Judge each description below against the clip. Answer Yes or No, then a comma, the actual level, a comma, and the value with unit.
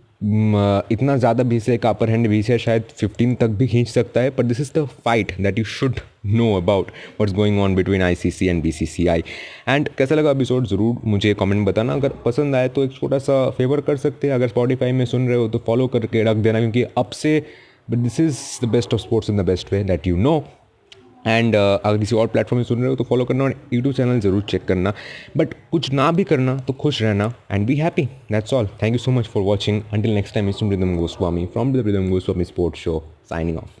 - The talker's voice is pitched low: Yes, low, 115 Hz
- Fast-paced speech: Yes, fast, 240 wpm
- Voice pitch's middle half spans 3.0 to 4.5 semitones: Yes, average, 3.8 semitones